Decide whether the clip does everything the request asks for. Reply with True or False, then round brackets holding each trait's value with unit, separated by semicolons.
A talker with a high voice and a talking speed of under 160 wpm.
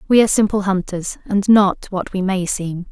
False (195 Hz; 205 wpm)